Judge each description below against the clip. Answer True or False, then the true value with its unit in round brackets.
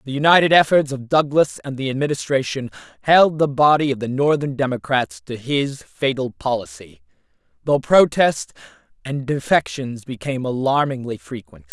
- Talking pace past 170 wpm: False (135 wpm)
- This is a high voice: False (135 Hz)